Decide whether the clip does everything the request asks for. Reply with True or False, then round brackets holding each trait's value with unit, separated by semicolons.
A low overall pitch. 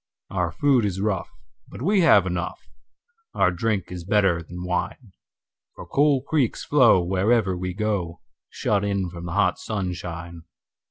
True (95 Hz)